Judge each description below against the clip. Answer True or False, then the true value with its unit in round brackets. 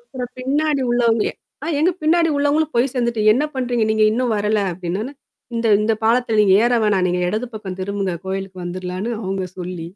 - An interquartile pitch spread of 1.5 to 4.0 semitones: False (4.9 semitones)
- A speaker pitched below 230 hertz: True (220 Hz)